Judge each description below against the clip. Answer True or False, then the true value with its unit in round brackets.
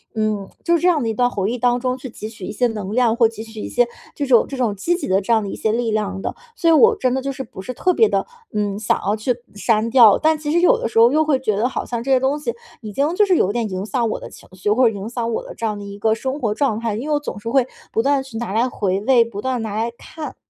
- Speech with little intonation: False (3.8 semitones)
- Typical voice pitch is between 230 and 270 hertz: True (235 Hz)